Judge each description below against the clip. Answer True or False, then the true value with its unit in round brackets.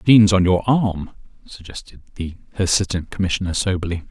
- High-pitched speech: False (95 Hz)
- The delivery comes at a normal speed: True (145 wpm)